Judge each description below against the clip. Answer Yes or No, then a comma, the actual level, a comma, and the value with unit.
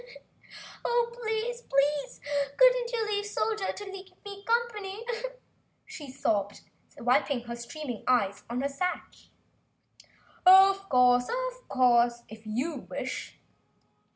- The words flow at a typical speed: No, slow, 110 wpm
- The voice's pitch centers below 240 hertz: No, very high, 360 Hz